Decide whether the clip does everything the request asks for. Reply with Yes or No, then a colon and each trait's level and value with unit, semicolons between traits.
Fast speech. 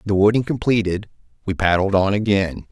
No: average, 155 wpm